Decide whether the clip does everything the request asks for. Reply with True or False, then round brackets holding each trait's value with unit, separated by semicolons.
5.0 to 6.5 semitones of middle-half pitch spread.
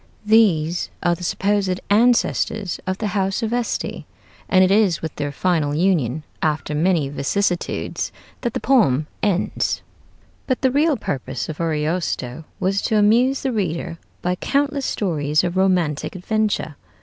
True (5.4 semitones)